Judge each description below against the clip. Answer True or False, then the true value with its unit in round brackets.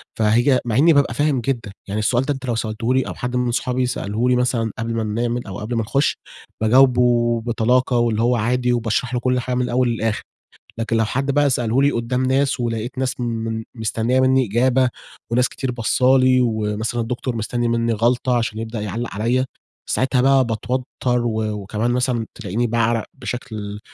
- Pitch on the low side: True (120 Hz)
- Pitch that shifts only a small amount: True (2.1 semitones)